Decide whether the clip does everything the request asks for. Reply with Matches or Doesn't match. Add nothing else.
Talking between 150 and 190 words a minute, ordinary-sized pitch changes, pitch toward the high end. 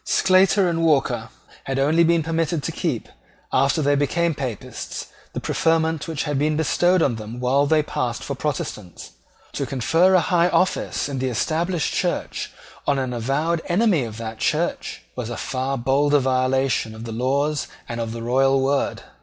Doesn't match